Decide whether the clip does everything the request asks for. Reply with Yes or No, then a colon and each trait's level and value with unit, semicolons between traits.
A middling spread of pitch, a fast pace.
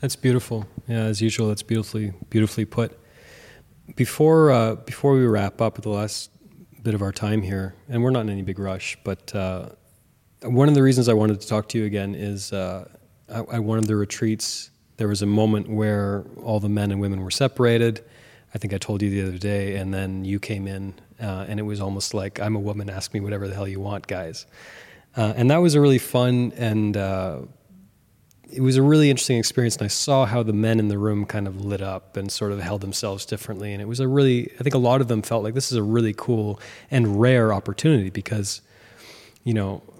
Yes: average, 3.0 semitones; fast, 225 wpm